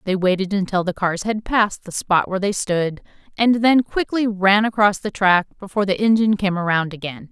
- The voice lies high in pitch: Yes, high, 200 Hz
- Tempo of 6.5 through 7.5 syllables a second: No, 5.5 syllables/s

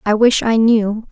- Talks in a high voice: Yes, high, 220 Hz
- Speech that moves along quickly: Yes, fast, 215 wpm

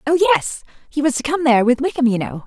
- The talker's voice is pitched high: Yes, very high, 260 Hz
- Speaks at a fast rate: Yes, fast, 245 wpm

